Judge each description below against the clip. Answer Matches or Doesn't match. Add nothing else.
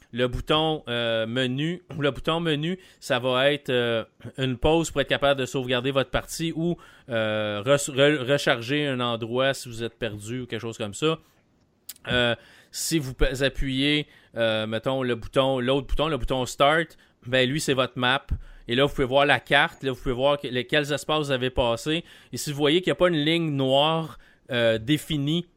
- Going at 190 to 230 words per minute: Matches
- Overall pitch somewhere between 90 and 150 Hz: Matches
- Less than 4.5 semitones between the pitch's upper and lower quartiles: Matches